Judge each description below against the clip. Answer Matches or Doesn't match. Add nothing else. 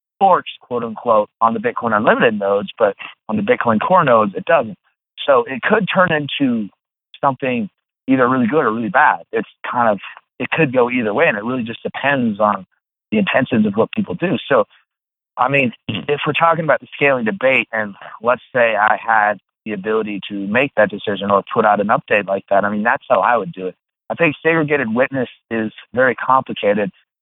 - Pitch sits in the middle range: Doesn't match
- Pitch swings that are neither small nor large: Doesn't match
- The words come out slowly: Doesn't match